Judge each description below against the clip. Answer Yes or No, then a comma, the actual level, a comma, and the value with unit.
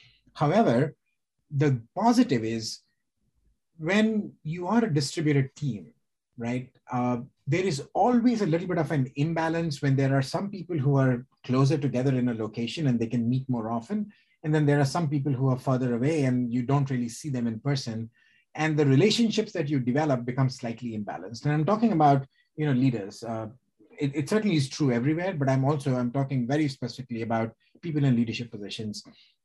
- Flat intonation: No, average, 4.2 semitones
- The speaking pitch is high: No, low, 135 Hz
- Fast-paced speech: No, average, 185 wpm